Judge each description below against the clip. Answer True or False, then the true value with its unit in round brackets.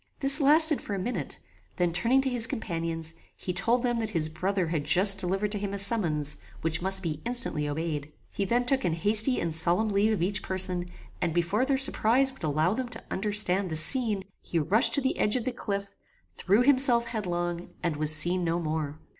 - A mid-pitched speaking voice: False (195 Hz)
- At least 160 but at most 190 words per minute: False (205 wpm)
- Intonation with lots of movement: True (5.8 semitones)